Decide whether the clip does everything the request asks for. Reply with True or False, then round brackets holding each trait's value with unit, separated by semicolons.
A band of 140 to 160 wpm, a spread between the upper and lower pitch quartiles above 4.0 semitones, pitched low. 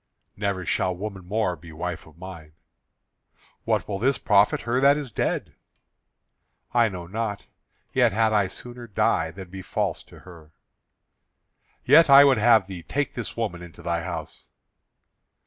True (155 wpm; 4.7 semitones; 100 Hz)